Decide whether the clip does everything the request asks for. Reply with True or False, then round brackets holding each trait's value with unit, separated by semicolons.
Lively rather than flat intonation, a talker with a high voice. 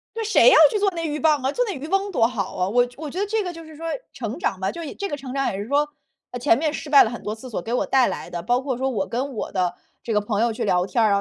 True (6.3 semitones; 260 Hz)